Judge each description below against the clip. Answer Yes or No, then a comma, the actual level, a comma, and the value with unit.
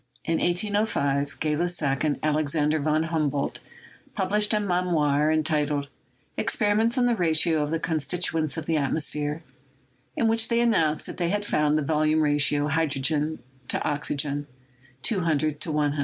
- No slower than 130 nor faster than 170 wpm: Yes, average, 140 wpm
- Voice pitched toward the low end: No, medium, 155 Hz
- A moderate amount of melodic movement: Yes, average, 3.2 semitones